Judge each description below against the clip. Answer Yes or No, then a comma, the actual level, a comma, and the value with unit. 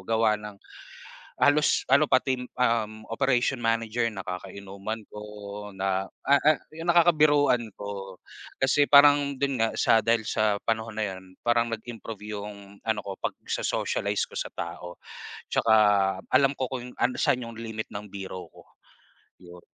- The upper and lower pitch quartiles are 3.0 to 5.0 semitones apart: Yes, average, 4.2 semitones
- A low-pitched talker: Yes, low, 115 Hz